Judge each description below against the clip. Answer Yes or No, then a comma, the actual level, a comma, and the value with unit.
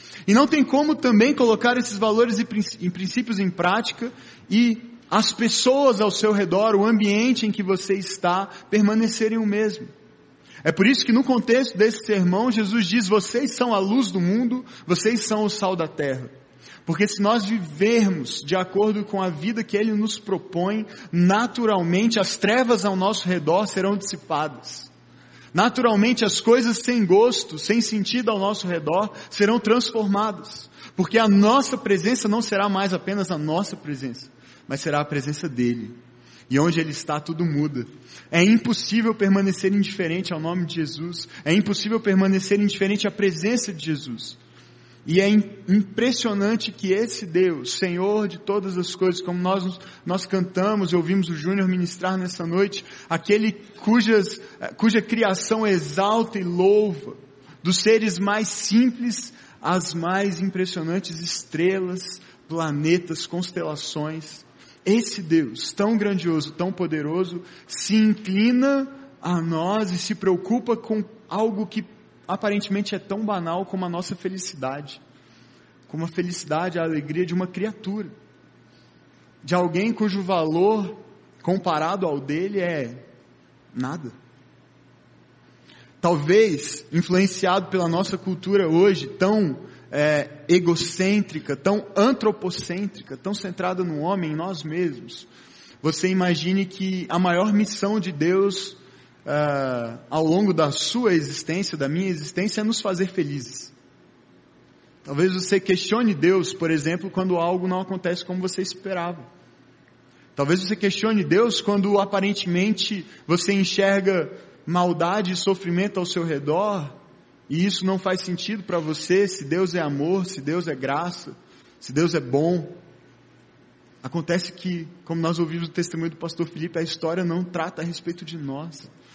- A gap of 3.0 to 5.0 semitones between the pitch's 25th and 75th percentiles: Yes, average, 3.7 semitones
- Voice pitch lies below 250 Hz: Yes, high, 190 Hz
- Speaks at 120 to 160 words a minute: Yes, average, 140 wpm